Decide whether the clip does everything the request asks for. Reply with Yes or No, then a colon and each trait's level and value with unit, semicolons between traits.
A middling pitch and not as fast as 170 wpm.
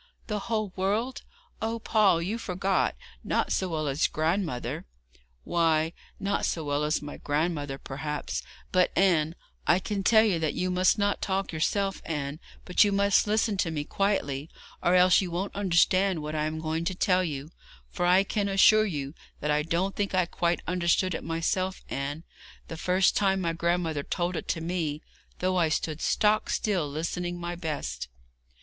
No: medium, 175 Hz; average, 180 wpm